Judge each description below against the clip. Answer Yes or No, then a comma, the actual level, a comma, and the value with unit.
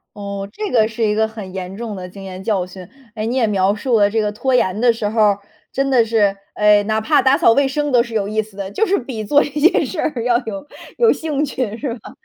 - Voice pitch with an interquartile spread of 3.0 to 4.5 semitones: Yes, average, 4.2 semitones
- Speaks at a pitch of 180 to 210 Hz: No, high, 220 Hz